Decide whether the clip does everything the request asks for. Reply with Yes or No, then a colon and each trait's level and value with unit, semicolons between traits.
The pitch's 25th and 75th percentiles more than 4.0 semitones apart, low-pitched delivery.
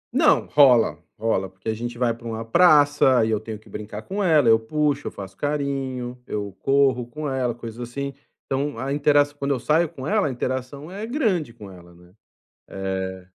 Yes: average, 4.6 semitones; low, 125 Hz